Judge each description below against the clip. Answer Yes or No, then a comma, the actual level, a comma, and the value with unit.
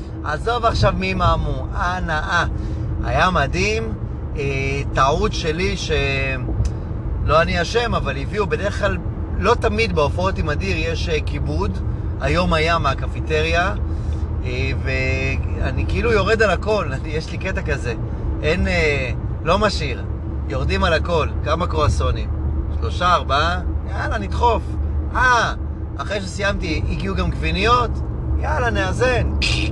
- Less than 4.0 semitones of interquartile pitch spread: Yes, average, 2.9 semitones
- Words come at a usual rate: Yes, average, 125 wpm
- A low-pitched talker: Yes, very low, 80 Hz